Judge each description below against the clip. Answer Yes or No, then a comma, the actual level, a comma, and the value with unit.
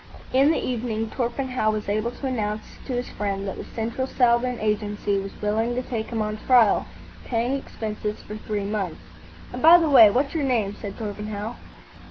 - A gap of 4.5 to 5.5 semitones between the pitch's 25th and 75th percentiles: No, average, 3.1 semitones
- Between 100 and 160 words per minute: No, average, 185 wpm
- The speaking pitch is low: No, high, 225 Hz